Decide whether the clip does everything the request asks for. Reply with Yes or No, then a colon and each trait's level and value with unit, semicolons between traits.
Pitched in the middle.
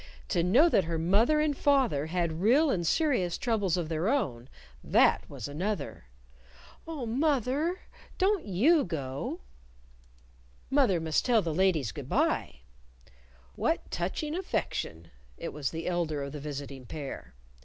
Yes: medium, 180 Hz